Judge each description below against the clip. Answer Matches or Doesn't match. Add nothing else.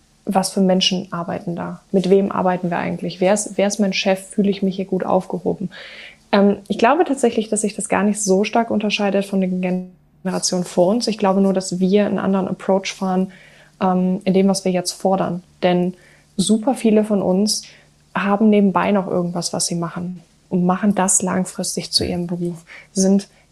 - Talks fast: Matches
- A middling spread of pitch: Doesn't match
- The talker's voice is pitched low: Doesn't match